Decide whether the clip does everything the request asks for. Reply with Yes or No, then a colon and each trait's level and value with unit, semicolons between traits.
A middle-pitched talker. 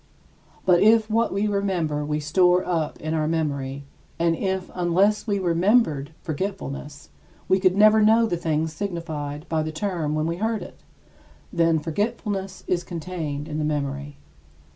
Yes: medium, 170 Hz